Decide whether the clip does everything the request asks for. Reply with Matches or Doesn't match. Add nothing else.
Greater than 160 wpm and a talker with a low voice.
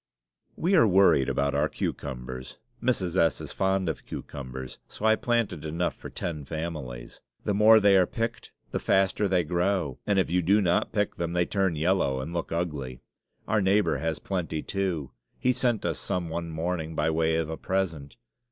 Matches